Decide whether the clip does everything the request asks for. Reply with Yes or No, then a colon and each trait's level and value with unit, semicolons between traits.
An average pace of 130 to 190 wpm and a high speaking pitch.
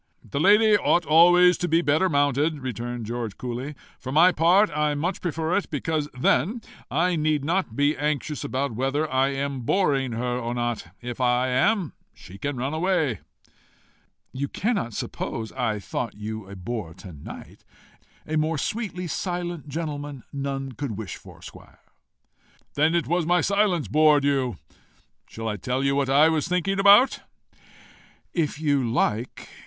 No: average, 160 wpm; medium, 145 Hz